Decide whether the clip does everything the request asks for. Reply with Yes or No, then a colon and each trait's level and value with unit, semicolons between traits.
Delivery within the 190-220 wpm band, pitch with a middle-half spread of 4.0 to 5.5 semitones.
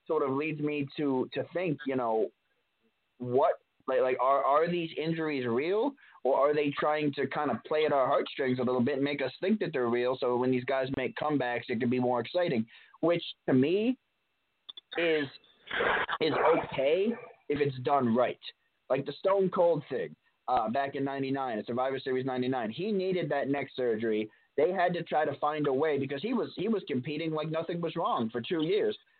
Yes: average, 200 wpm; average, 4.4 semitones